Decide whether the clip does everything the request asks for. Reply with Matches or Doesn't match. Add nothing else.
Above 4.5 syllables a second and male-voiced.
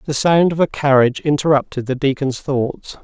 Matches